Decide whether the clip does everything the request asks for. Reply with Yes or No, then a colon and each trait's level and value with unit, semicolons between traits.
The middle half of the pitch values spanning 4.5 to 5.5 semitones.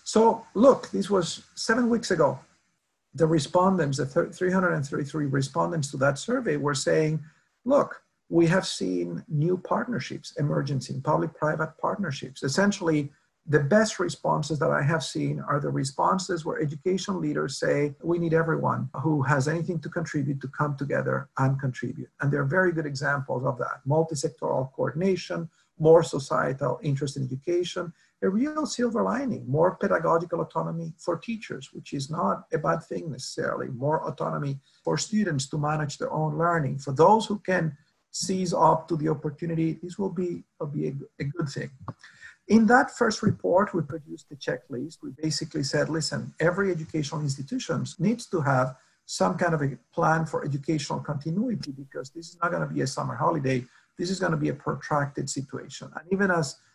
No: average, 3.8 semitones